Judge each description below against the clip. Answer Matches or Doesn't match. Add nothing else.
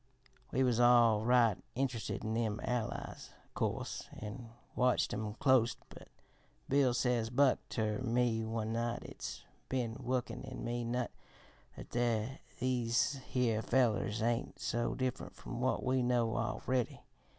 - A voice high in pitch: Doesn't match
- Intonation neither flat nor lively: Doesn't match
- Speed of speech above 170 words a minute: Doesn't match